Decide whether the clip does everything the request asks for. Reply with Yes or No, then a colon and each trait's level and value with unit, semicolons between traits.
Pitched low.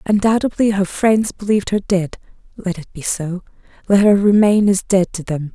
No: high, 195 Hz